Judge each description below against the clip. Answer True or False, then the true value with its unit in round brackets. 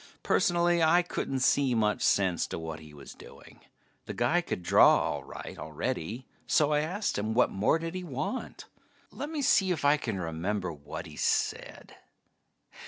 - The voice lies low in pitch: True (125 Hz)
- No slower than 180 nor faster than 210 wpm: False (170 wpm)